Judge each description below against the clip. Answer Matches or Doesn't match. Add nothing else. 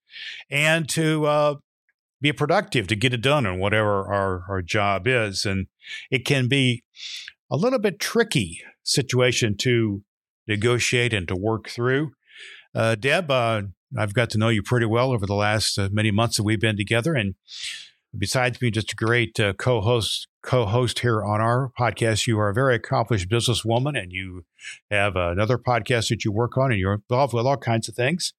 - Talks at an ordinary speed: Matches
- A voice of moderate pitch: Doesn't match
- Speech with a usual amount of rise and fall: Matches